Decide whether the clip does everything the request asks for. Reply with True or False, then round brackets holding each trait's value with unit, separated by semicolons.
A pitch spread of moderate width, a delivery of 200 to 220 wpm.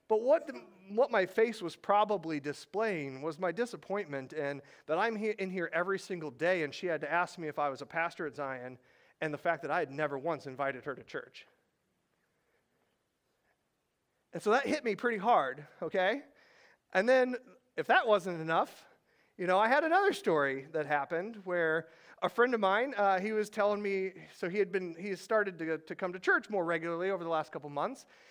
True (4.9 semitones; 205 wpm)